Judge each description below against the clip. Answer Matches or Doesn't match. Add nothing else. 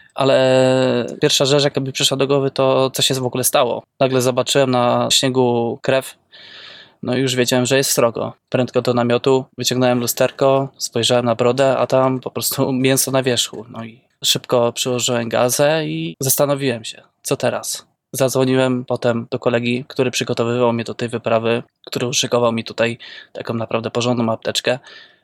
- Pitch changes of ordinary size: Doesn't match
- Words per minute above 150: Matches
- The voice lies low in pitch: Matches